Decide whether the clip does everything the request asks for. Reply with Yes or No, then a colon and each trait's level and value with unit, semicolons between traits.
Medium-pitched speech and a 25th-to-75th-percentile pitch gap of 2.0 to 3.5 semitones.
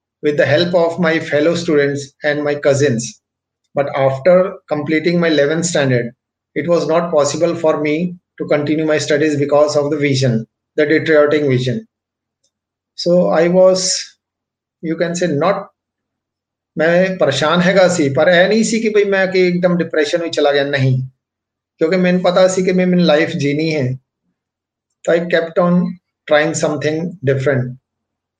No: medium, 150 Hz; average, 4.1 semitones